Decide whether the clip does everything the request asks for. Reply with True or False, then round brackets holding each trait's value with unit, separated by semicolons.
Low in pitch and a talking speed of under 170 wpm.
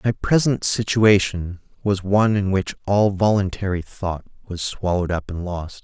True (95 Hz; 155 wpm)